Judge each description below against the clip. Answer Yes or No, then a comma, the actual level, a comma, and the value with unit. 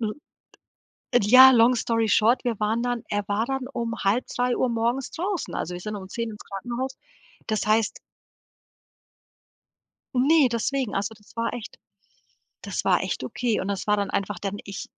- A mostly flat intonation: No, average, 3.1 semitones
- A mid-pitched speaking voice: No, high, 230 Hz